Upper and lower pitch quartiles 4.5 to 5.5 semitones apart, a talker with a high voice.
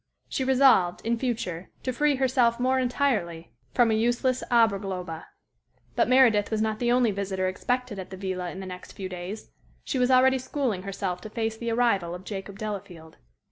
Yes: average, 5.0 semitones; high, 220 Hz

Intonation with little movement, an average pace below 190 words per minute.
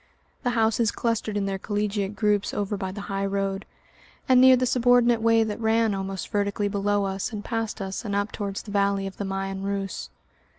No: narrow, 2.3 semitones; average, 200 wpm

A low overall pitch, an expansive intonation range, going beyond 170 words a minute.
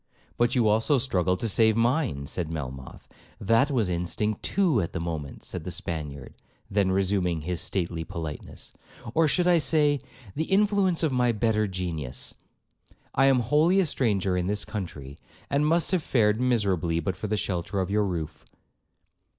No: low, 105 Hz; wide, 7.4 semitones; average, 165 wpm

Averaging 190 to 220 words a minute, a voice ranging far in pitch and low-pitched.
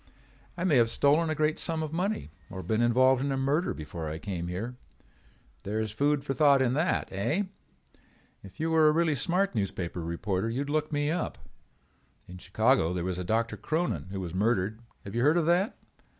Yes: fast, 205 wpm; wide, 8.0 semitones; low, 125 Hz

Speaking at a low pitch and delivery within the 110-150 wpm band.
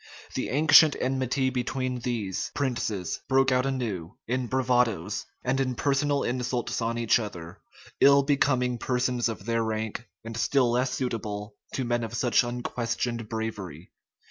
Yes: low, 120 Hz; average, 145 wpm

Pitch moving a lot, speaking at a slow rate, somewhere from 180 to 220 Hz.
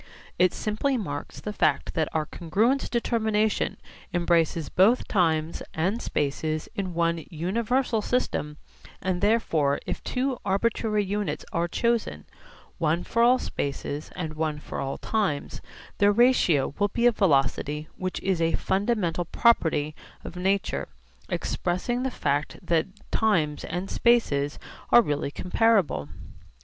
Yes: wide, 6.0 semitones; slow, 130 wpm; medium, 185 Hz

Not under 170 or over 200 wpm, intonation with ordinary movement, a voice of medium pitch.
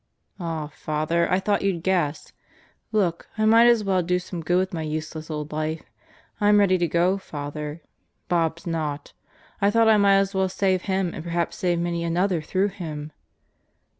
Yes: average, 175 wpm; average, 3.4 semitones; medium, 175 Hz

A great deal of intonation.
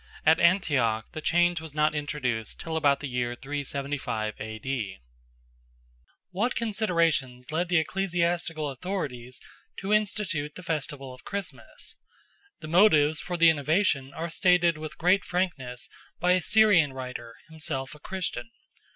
No: average, 4.9 semitones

